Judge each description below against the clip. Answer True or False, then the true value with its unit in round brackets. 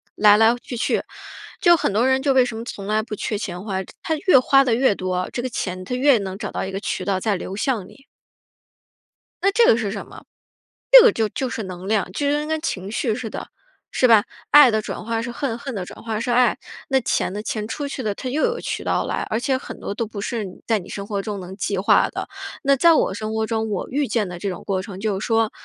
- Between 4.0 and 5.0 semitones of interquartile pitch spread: True (4.5 semitones)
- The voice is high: True (220 Hz)